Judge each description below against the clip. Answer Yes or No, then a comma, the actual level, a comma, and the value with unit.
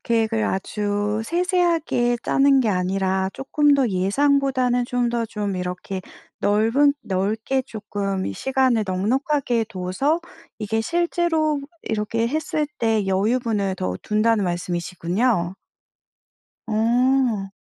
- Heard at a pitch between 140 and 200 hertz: No, high, 225 Hz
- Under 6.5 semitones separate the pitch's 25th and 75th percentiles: Yes, wide, 5.4 semitones